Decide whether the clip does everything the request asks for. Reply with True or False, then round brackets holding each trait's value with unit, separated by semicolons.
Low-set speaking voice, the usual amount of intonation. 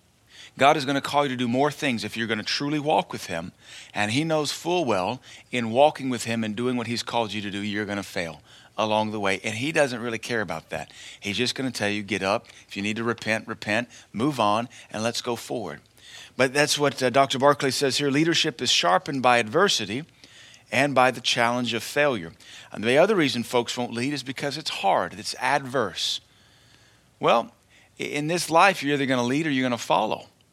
True (125 Hz; 4.2 semitones)